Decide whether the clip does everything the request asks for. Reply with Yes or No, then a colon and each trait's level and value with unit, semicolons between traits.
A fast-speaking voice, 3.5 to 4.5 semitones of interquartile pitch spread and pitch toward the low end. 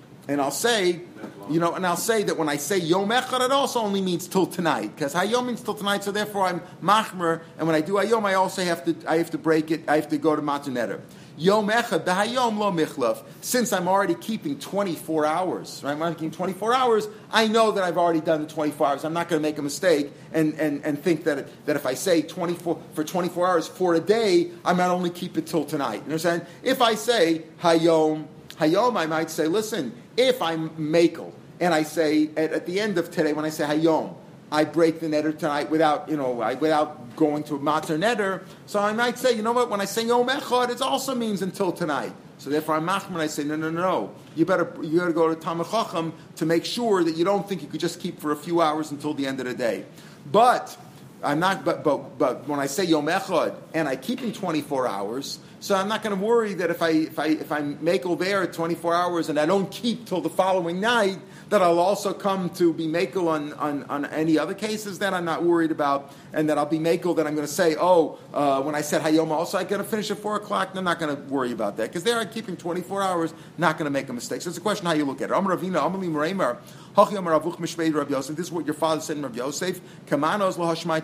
No: fast, 245 wpm; average, 3.9 semitones; medium, 170 Hz